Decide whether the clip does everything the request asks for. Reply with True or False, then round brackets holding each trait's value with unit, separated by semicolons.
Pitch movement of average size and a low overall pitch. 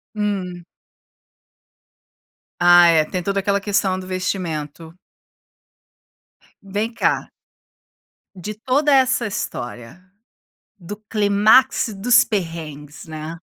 False (3.8 semitones; 185 Hz)